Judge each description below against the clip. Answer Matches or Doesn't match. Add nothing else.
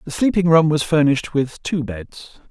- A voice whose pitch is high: Doesn't match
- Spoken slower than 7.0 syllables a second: Matches